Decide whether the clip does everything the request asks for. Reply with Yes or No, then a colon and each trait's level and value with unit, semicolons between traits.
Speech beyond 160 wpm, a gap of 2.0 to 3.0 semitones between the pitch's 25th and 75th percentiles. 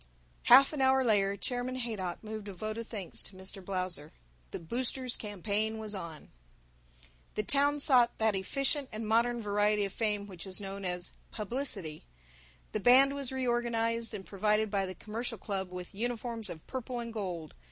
No: average, 170 wpm; average, 3.7 semitones